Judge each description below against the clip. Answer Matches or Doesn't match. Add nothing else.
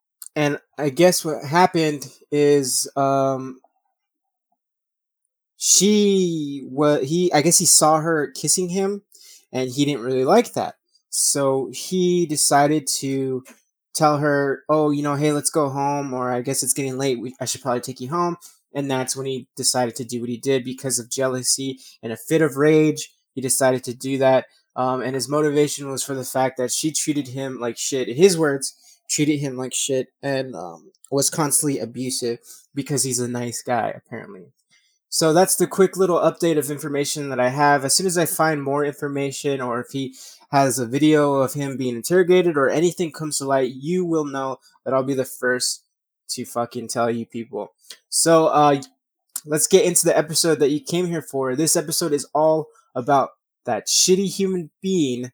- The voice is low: Doesn't match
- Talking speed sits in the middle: Matches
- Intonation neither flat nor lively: Matches